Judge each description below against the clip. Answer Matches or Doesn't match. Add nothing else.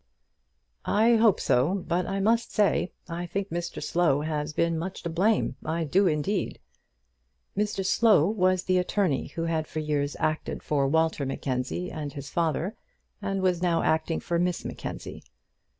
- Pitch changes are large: Doesn't match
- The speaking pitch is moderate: Matches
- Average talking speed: Matches